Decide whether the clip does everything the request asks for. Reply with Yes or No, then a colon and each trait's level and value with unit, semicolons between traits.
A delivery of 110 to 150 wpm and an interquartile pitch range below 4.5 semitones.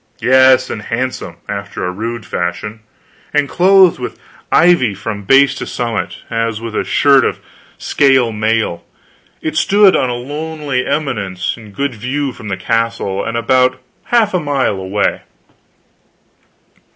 No: average, 140 wpm; average, 4.8 semitones